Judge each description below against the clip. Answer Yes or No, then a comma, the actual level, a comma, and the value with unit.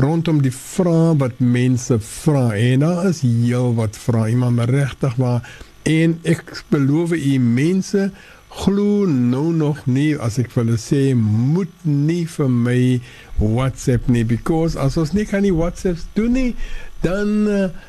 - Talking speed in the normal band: Yes, average, 150 wpm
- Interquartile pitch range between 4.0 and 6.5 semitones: Yes, wide, 5.6 semitones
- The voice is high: No, medium, 140 Hz